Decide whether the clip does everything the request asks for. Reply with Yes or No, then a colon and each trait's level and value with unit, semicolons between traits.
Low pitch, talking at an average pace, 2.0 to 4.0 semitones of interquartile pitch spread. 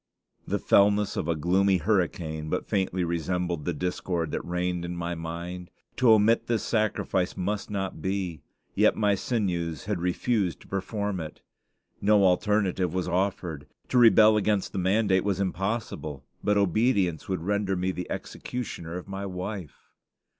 Yes: very low, 95 Hz; average, 155 wpm; average, 2.9 semitones